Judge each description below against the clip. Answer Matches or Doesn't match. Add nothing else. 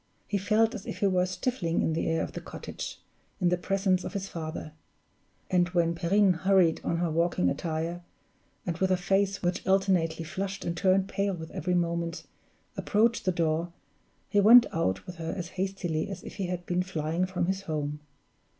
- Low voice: Doesn't match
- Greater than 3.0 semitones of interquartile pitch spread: Doesn't match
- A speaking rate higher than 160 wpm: Matches